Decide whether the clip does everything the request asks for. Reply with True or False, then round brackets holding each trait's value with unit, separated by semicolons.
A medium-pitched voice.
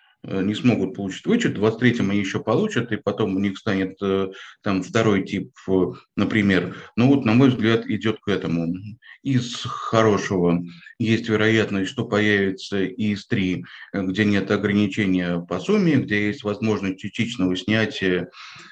False (105 Hz)